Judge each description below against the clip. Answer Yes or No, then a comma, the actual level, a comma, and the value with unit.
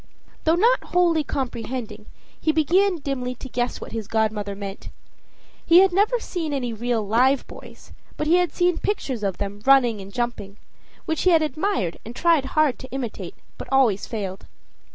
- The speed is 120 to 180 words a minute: Yes, average, 175 wpm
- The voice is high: Yes, very high, 265 Hz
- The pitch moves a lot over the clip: Yes, wide, 6.7 semitones